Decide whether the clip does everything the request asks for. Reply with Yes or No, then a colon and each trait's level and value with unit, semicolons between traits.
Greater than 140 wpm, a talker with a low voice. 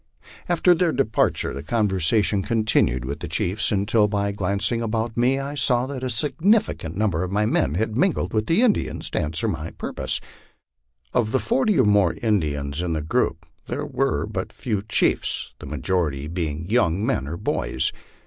Yes: average, 175 wpm; low, 105 Hz